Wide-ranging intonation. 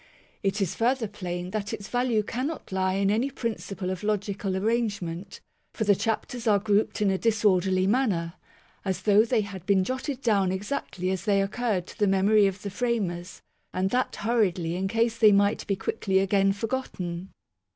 No: average, 2.9 semitones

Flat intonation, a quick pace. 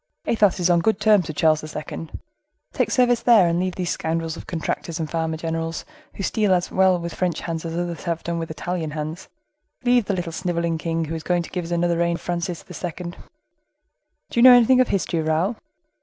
Yes: narrow, 2.3 semitones; fast, 215 wpm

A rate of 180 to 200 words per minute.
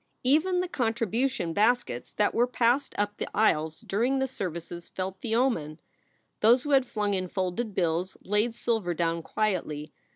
Yes: average, 185 wpm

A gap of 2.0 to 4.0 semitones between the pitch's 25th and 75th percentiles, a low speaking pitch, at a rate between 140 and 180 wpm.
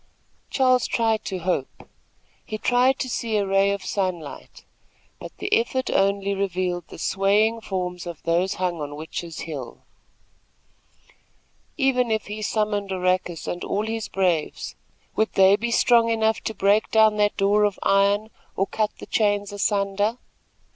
No: average, 2.9 semitones; high, 200 Hz; average, 150 wpm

